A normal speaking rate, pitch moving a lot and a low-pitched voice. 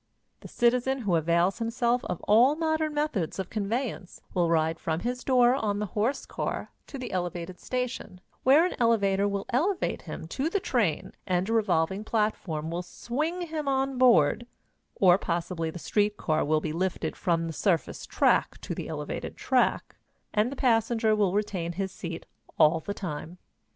No: average, 170 wpm; wide, 6.2 semitones; high, 210 Hz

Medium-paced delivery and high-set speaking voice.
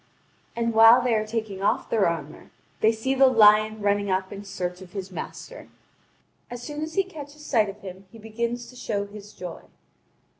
Yes: average, 190 wpm; high, 215 Hz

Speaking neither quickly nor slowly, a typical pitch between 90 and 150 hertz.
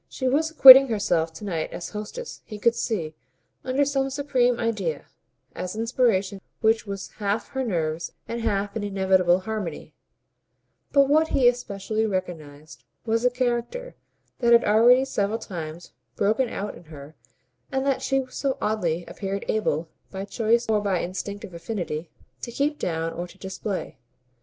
No: average, 155 wpm; high, 215 Hz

